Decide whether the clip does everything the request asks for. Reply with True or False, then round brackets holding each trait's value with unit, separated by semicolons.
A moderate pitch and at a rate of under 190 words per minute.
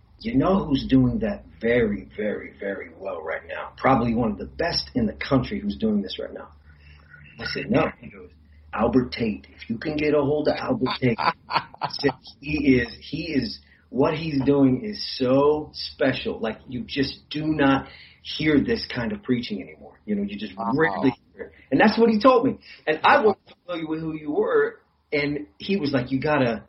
False (150 Hz; 200 wpm)